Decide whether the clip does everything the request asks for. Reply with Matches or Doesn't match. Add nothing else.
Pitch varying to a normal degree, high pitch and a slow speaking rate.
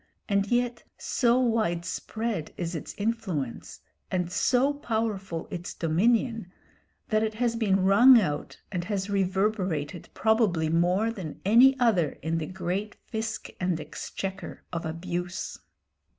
Matches